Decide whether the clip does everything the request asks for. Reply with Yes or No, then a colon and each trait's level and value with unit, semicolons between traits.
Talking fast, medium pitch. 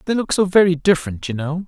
Yes: fast, 250 wpm; medium, 170 Hz